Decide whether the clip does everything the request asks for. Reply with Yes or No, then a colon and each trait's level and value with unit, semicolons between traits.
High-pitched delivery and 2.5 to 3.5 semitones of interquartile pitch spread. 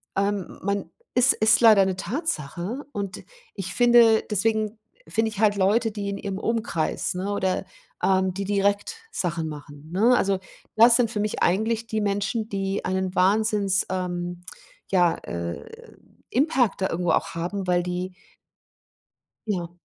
Yes: high, 200 Hz; average, 3.2 semitones